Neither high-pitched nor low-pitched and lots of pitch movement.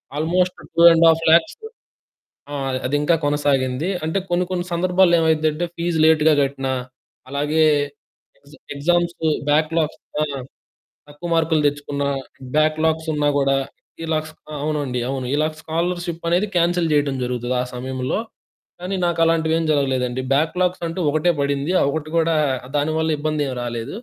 No: medium, 155 Hz; average, 2.7 semitones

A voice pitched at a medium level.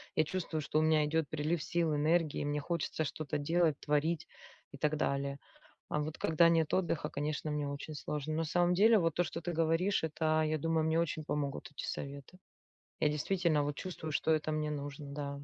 Yes: medium, 155 Hz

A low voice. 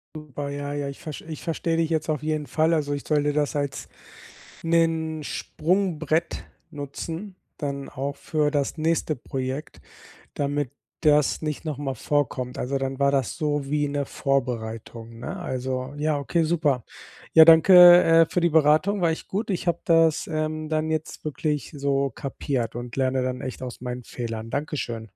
No: medium, 145 Hz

